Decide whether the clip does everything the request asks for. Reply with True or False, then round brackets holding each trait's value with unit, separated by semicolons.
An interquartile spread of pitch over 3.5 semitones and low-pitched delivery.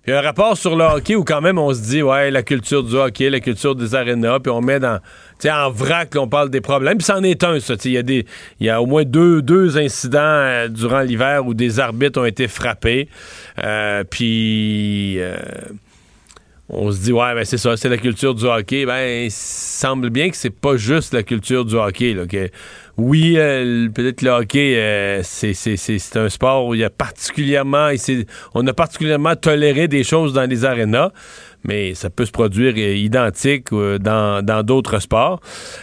True (4.0 semitones; 125 Hz)